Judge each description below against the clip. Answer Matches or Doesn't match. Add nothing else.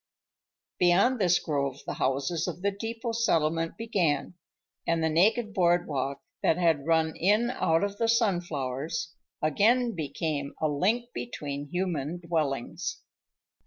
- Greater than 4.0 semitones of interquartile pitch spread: Matches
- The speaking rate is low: Matches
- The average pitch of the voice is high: Doesn't match